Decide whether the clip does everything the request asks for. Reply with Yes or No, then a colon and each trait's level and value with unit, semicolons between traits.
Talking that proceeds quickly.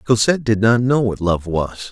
Yes: fast, 220 wpm